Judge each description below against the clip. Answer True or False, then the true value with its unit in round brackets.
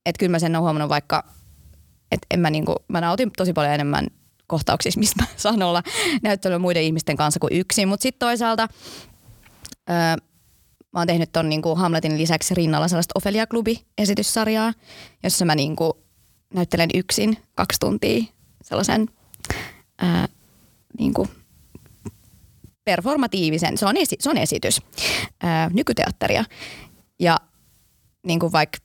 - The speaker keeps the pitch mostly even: False (5.0 semitones)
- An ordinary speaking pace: True (130 wpm)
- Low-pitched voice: False (170 Hz)